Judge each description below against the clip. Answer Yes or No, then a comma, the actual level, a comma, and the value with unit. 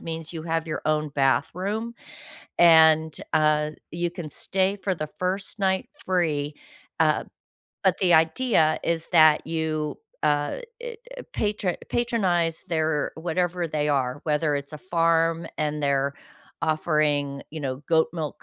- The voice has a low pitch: No, medium, 160 Hz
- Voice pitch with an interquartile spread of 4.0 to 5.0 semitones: No, narrow, 2.6 semitones